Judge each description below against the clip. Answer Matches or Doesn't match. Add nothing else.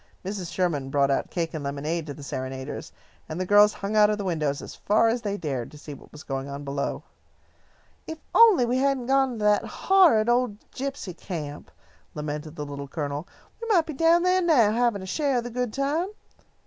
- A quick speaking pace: Matches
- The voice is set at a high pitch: Matches